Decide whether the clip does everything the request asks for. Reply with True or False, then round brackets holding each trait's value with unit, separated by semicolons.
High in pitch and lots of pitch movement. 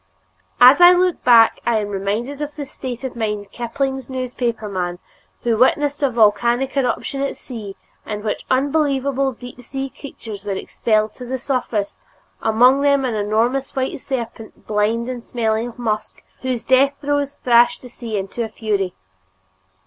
False (240 Hz; 3.6 semitones)